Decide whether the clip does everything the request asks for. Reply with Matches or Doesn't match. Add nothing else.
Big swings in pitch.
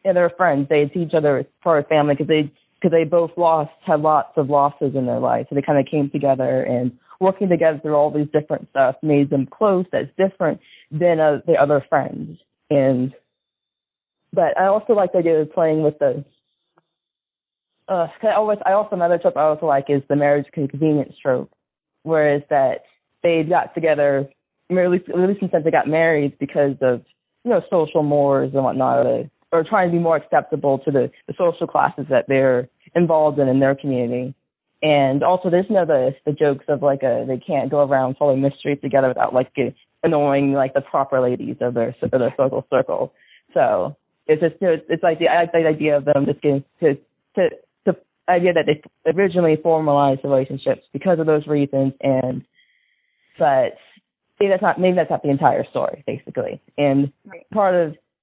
Doesn't match